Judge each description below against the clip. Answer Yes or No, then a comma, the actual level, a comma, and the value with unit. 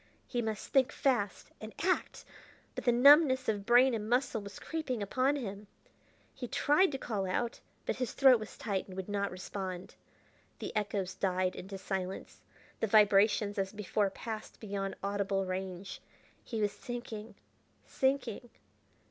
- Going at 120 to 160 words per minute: Yes, average, 150 wpm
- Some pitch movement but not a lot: Yes, average, 3.9 semitones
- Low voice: No, high, 210 Hz